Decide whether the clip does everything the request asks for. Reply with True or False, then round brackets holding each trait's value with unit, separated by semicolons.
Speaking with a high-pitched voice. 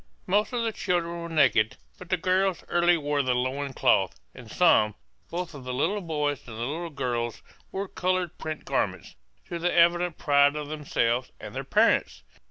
False (155 Hz)